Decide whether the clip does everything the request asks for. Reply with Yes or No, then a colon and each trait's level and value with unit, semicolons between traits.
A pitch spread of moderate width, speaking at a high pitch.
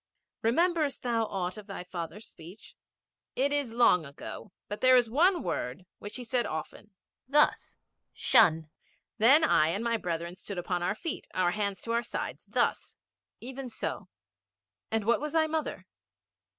No: wide, 6.4 semitones; high, 225 Hz